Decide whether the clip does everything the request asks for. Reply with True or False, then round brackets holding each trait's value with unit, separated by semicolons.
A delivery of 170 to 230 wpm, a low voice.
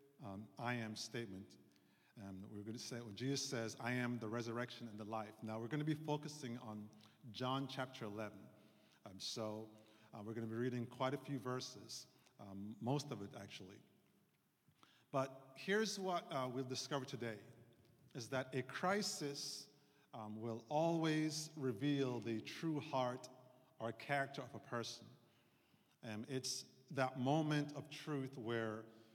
False (160 wpm; 125 Hz)